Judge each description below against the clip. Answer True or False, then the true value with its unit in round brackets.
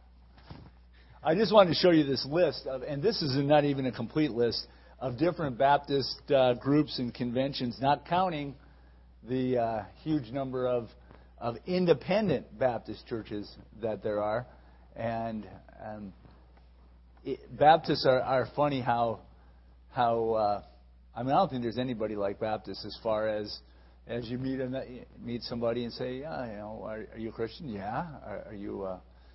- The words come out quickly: False (170 wpm)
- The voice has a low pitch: True (115 Hz)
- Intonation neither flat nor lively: False (7.2 semitones)